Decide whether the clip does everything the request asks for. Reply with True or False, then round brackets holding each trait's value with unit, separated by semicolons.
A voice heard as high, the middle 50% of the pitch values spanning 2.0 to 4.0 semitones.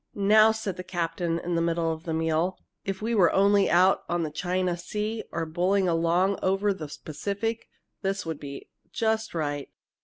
False (180 Hz; 3.4 semitones)